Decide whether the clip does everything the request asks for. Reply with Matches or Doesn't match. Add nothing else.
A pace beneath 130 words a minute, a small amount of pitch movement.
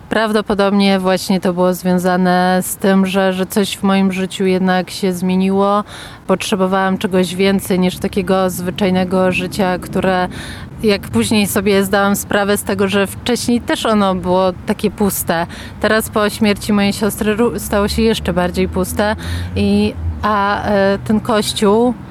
Doesn't match